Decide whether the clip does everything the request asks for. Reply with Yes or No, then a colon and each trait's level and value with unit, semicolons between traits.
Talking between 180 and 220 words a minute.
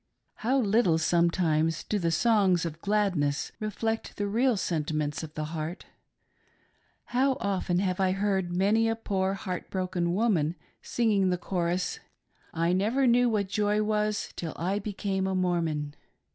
No: average, 150 wpm